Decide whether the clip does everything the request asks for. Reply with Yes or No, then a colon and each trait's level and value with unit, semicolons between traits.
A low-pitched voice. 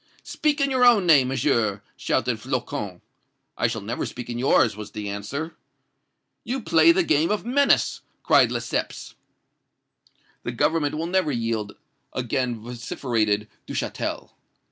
Yes: low, 130 Hz